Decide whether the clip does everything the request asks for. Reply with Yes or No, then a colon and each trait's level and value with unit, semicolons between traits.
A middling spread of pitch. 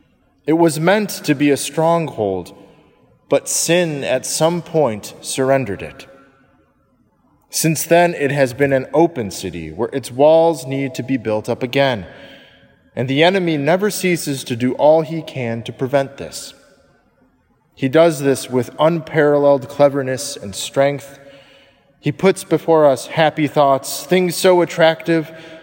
Yes: average, 3.4 semitones